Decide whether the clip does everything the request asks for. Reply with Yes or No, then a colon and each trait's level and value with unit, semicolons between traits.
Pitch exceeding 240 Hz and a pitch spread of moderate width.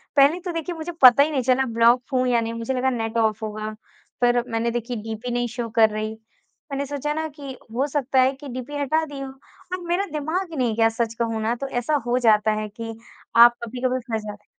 Yes: very high, 250 Hz; average, 3.8 semitones